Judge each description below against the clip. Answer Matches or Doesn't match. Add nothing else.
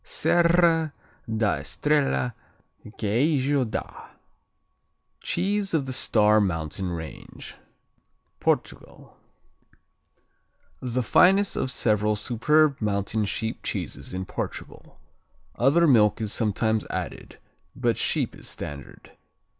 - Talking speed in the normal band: Doesn't match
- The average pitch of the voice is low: Matches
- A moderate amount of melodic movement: Doesn't match